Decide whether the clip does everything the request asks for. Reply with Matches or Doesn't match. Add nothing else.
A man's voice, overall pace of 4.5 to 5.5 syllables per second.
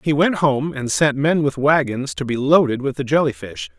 Matches